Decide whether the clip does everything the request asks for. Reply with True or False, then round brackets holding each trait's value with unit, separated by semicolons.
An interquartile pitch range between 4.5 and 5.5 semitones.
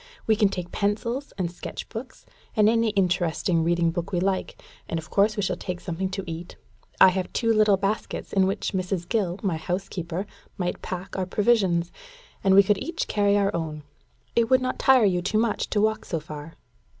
False (3.4 semitones)